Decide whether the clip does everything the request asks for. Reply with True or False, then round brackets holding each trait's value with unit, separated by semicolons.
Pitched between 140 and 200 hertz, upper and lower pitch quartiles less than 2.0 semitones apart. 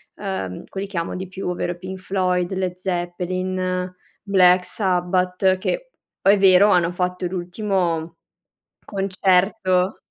True (185 Hz; 1.2 semitones)